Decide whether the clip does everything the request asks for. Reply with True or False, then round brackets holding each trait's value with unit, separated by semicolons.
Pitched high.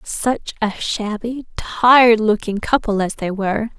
True (220 Hz)